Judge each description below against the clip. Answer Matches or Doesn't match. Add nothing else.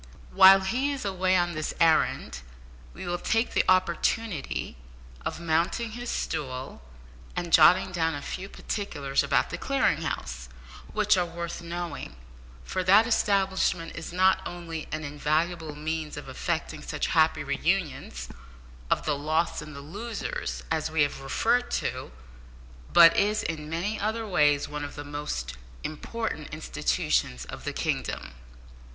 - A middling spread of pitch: Matches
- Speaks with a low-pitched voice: Doesn't match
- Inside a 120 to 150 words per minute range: Matches